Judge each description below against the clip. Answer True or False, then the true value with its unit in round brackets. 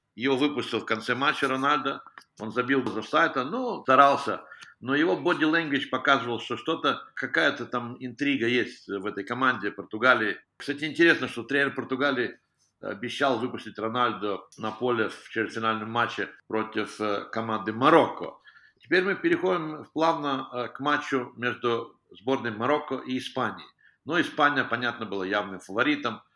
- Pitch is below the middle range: True (125 Hz)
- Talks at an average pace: True (135 wpm)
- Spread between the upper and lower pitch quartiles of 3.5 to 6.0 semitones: True (4.0 semitones)